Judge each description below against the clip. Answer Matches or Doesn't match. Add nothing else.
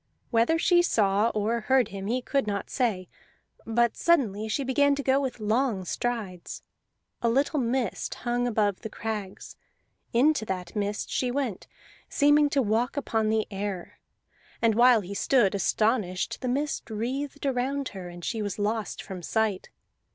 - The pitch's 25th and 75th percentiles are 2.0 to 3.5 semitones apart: Doesn't match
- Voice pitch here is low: Doesn't match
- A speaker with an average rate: Matches